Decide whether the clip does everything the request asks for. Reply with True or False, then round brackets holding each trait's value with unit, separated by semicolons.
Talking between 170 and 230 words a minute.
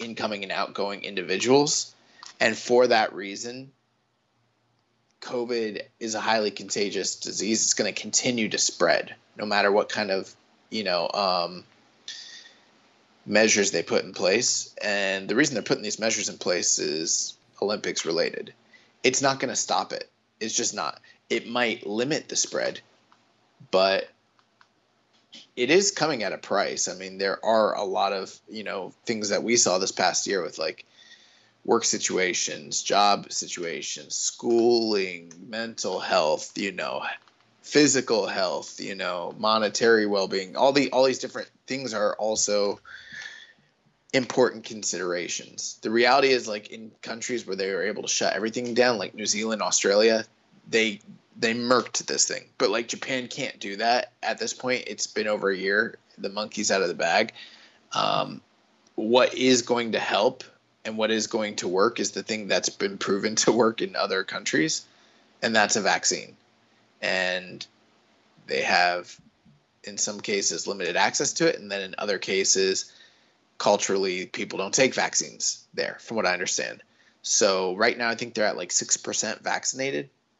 False (160 wpm)